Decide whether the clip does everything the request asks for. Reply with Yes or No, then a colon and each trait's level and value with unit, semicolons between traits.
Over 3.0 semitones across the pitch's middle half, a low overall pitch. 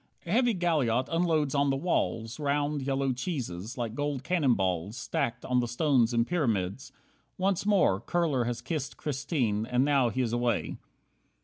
Yes: average, 4.3 semitones; low, 130 Hz